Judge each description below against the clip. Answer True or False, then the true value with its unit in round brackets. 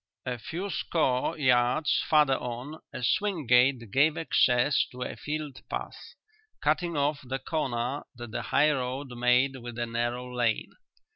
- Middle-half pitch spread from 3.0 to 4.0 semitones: True (3.5 semitones)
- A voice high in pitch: False (130 Hz)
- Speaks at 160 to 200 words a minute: False (150 wpm)